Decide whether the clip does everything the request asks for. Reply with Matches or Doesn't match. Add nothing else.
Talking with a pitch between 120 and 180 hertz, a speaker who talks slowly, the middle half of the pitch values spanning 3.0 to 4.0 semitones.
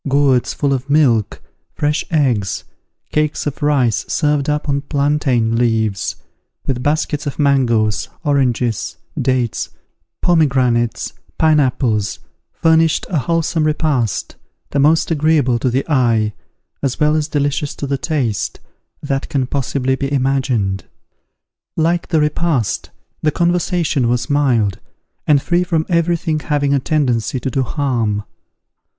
Matches